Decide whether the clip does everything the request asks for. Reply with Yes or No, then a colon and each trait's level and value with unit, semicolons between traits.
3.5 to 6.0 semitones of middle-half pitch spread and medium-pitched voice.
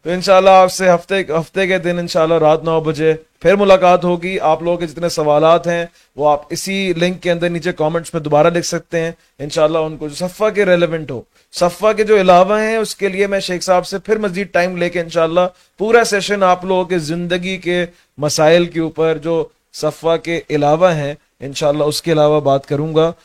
No: narrow, 2.6 semitones; medium, 175 Hz